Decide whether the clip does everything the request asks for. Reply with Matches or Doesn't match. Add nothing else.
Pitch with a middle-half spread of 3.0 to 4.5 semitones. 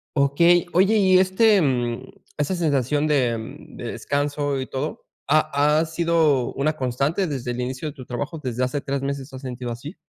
Matches